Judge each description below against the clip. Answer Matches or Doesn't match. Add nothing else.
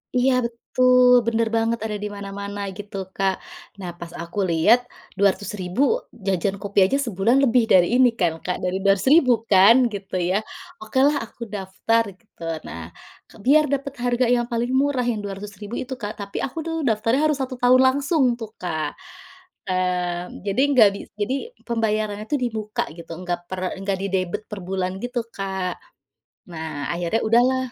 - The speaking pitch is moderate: Doesn't match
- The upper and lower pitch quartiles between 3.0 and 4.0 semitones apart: Doesn't match